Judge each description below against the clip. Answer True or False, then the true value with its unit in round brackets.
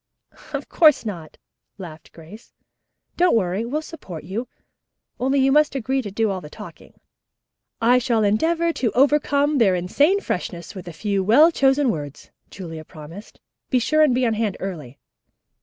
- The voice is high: True (225 Hz)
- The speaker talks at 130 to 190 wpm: True (160 wpm)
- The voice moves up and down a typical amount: False (7.4 semitones)